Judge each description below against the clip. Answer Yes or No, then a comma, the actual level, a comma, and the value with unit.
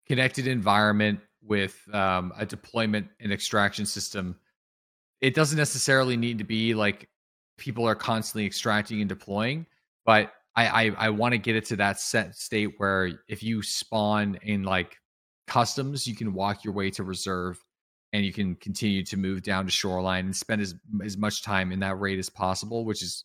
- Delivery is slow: No, average, 180 wpm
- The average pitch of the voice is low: Yes, low, 105 Hz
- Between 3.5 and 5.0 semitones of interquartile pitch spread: No, narrow, 2.6 semitones